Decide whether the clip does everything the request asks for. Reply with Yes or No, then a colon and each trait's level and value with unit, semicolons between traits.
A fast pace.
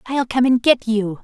Yes: fast, 245 wpm